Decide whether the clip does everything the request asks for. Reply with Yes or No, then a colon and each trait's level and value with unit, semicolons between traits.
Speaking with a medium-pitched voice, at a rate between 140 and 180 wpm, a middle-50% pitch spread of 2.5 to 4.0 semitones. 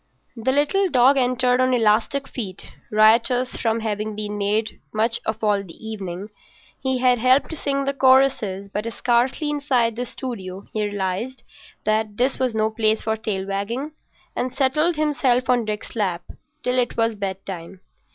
No: high, 230 Hz; average, 160 wpm; average, 3.7 semitones